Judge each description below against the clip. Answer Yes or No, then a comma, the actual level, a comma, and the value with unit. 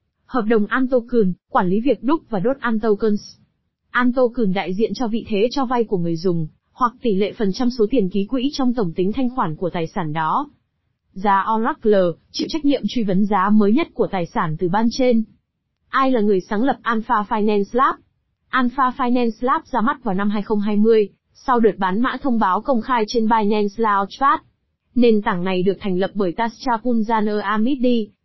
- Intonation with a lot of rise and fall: No, average, 3.7 semitones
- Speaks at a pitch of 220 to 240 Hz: Yes, high, 225 Hz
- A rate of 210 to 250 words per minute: No, average, 195 wpm